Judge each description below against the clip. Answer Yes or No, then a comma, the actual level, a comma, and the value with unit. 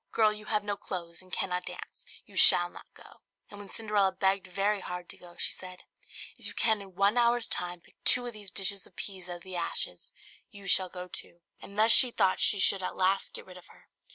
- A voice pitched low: No, high, 195 Hz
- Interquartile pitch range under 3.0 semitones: Yes, narrow, 2.5 semitones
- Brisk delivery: Yes, fast, 235 wpm